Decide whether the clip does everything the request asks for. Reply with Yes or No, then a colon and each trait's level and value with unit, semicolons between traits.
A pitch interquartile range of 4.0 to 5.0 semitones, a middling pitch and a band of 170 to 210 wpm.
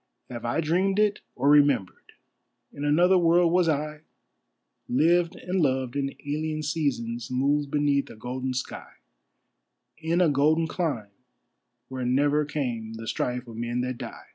No: average, 4.3 semitones; medium, 145 Hz; average, 145 wpm